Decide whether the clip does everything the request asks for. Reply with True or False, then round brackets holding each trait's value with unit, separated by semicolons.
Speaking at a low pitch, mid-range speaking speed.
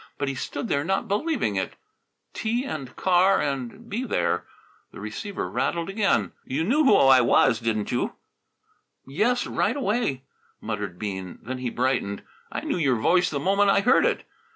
False (145 Hz; 170 wpm)